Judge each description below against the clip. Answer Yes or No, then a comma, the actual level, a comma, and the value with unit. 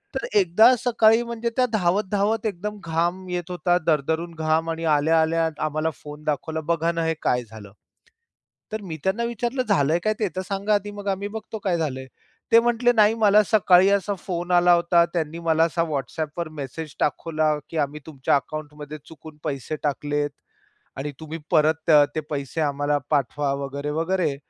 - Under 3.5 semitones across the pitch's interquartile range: No, average, 4.8 semitones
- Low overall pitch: No, medium, 165 Hz